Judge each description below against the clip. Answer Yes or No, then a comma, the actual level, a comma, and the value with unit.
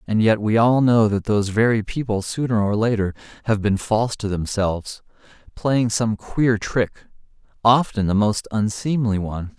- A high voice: No, low, 110 Hz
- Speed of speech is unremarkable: Yes, average, 165 wpm